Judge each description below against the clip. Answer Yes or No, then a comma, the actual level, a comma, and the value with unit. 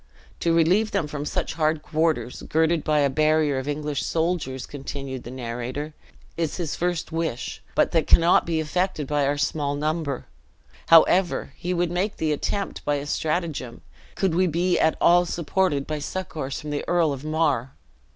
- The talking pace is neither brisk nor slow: Yes, average, 170 wpm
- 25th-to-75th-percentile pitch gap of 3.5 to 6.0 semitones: No, average, 2.9 semitones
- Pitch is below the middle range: No, medium, 155 Hz